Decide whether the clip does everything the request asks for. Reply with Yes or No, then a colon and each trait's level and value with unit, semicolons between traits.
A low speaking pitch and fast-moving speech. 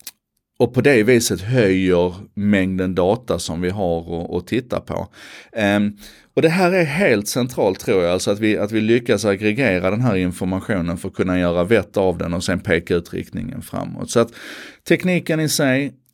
No: low, 105 Hz; average, 185 wpm